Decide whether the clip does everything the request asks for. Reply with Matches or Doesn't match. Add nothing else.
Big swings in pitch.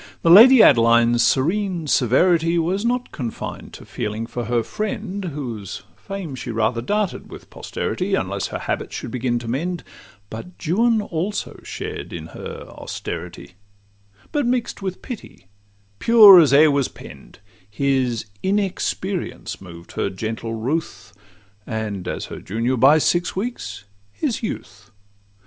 Matches